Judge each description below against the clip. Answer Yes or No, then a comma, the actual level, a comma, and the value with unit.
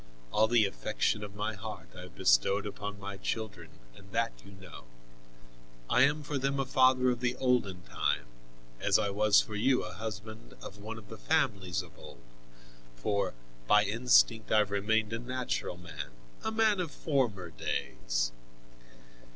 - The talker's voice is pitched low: Yes, low, 105 Hz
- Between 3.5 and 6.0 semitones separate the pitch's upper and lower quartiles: Yes, average, 4.4 semitones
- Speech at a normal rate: Yes, average, 165 wpm